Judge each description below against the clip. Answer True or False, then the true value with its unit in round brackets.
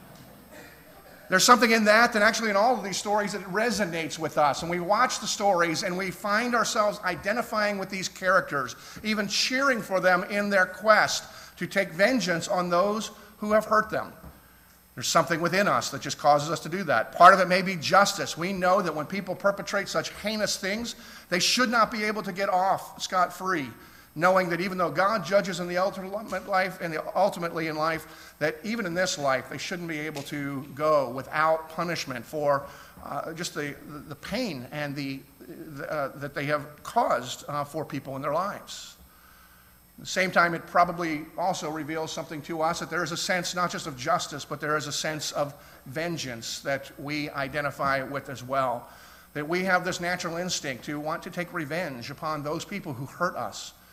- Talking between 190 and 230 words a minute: True (200 wpm)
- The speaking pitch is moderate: True (175 Hz)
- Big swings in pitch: False (4.7 semitones)